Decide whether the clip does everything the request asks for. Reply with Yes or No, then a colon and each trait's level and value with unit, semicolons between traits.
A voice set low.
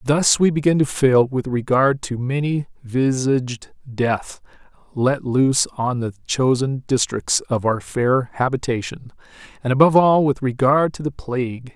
Yes: low, 130 Hz